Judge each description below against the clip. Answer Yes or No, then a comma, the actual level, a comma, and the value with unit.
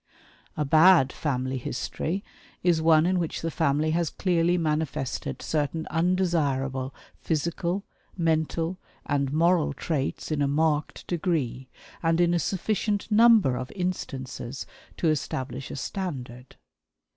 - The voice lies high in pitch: No, medium, 160 Hz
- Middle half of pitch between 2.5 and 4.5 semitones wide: Yes, average, 4.0 semitones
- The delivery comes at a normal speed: No, slow, 120 wpm